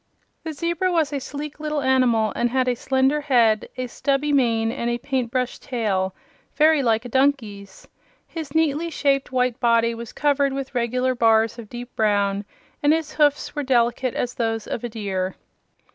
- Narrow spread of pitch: No, average, 3.7 semitones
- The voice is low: No, very high, 255 Hz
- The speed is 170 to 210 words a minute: Yes, average, 175 wpm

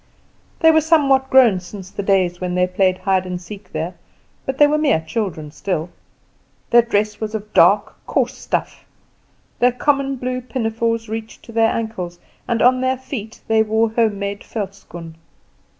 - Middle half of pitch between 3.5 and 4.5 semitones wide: No, average, 5.1 semitones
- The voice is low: No, high, 220 Hz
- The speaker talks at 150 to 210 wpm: Yes, average, 165 wpm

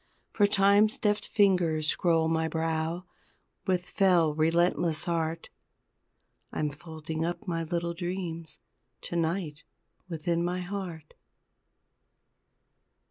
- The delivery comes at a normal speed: No, slow, 100 wpm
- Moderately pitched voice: Yes, medium, 170 Hz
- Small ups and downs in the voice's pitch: Yes, narrow, 2.1 semitones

